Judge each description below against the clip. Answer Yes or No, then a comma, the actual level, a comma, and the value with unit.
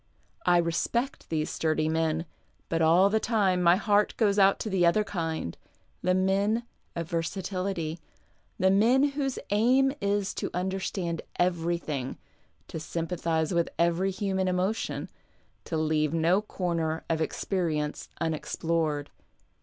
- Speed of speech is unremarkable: No, slow, 130 wpm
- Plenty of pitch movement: No, average, 3.4 semitones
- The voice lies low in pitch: No, medium, 175 Hz